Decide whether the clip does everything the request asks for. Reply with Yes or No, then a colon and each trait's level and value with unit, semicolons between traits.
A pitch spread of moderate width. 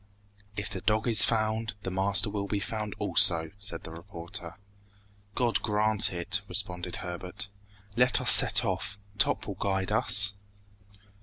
Yes: average, 3.0 semitones